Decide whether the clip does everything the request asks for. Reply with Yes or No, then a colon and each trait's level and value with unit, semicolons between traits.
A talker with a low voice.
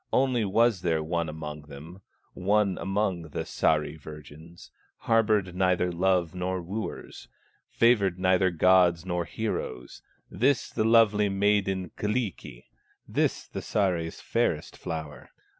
Yes: very low, 90 Hz